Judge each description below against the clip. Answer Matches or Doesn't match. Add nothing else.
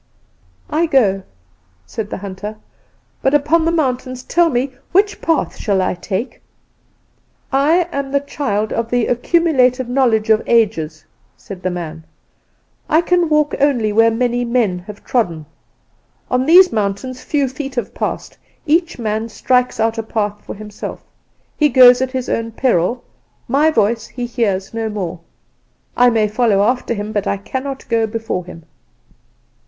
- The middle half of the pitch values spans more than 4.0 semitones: Matches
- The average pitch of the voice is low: Doesn't match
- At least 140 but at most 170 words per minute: Matches